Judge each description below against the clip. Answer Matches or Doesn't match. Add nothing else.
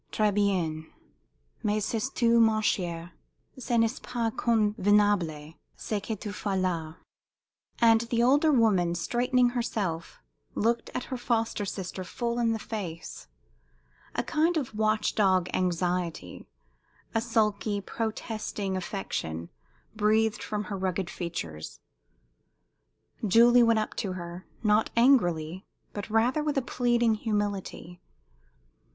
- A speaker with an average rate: Doesn't match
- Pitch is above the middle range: Matches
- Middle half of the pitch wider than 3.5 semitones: Matches